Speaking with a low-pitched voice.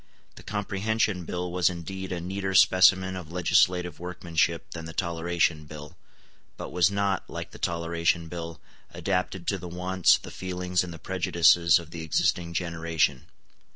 Yes: very low, 90 Hz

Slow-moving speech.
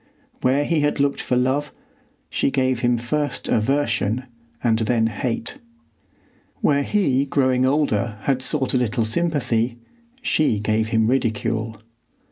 Yes: slow, 130 wpm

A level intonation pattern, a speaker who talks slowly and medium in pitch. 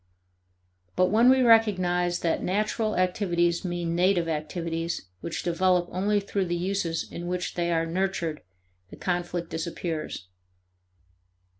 Yes: narrow, 2.1 semitones; slow, 125 wpm; medium, 175 Hz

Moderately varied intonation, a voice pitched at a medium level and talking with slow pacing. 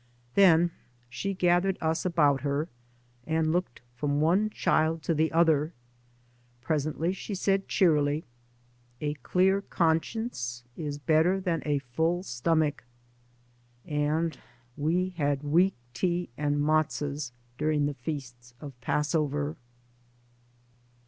Yes: average, 3.1 semitones; medium, 155 Hz; slow, 115 wpm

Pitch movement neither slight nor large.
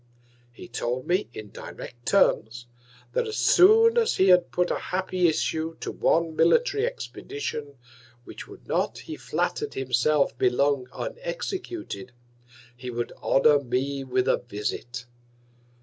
No: wide, 8.1 semitones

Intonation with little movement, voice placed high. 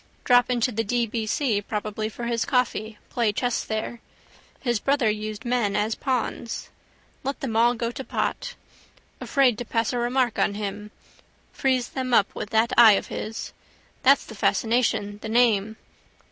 Yes: narrow, 2.3 semitones; high, 230 Hz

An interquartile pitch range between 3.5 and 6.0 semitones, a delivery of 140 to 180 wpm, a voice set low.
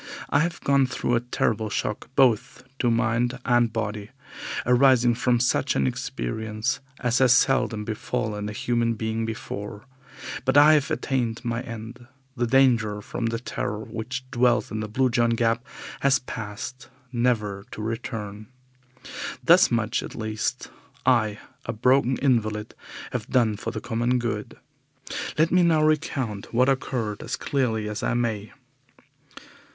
No: average, 2.8 semitones; average, 145 wpm; low, 115 Hz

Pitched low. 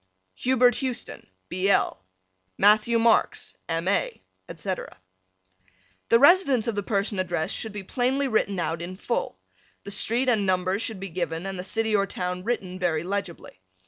No: high, 200 Hz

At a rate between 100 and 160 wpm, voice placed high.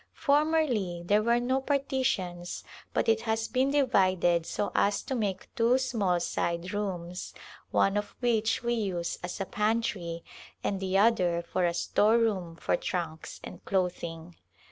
Yes: average, 150 wpm; high, 200 Hz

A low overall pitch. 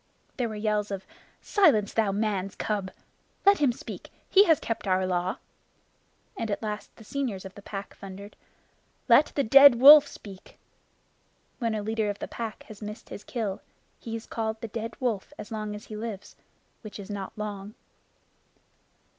No: high, 215 Hz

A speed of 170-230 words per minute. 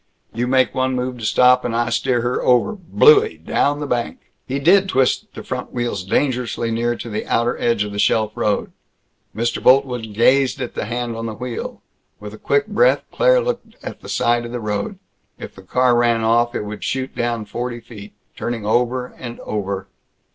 Yes: average, 200 wpm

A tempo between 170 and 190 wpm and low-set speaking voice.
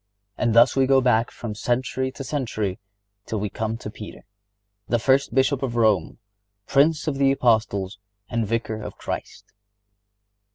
No: average, 155 wpm; low, 120 Hz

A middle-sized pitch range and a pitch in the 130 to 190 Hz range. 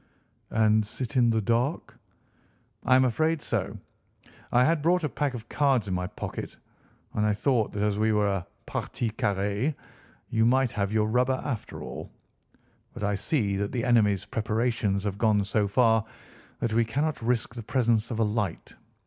No: average, 3.4 semitones; low, 115 Hz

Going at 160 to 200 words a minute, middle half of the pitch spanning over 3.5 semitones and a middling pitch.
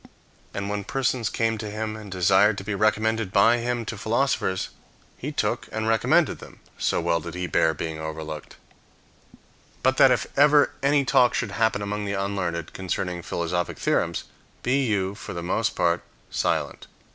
No: average, 170 wpm; average, 3.9 semitones; low, 105 Hz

